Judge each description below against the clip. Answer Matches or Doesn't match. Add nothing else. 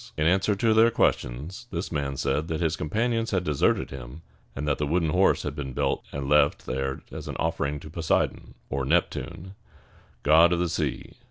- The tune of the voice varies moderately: Matches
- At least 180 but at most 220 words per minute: Matches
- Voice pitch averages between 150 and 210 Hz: Doesn't match